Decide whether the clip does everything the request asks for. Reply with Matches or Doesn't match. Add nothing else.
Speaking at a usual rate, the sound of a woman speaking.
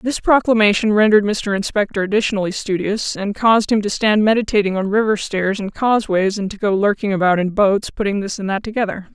Matches